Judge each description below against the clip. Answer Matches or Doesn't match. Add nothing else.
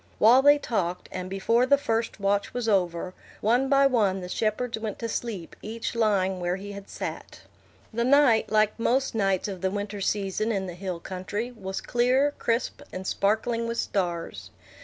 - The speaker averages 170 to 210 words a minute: Matches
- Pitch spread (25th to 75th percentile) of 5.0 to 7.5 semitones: Doesn't match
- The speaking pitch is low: Doesn't match